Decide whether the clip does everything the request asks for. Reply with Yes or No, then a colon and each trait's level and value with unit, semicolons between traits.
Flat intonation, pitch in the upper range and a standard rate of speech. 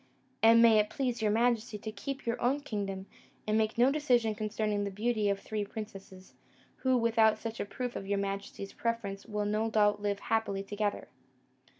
Yes: narrow, 2.3 semitones; high, 215 Hz; average, 185 wpm